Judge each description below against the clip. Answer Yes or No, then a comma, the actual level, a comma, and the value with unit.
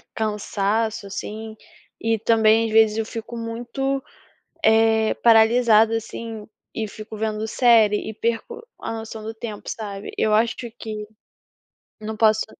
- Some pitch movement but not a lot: No, narrow, 1.0 semitones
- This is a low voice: No, high, 220 Hz